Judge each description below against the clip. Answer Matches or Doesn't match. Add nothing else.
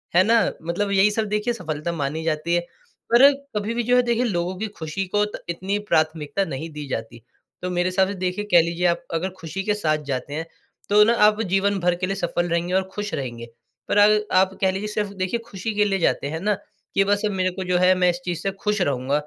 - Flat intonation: Doesn't match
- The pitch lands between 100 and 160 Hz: Doesn't match